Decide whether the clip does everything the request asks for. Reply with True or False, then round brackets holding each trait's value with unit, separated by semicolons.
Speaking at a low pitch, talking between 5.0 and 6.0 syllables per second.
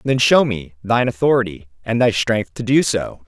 True (110 Hz; 5.1 syllables/s)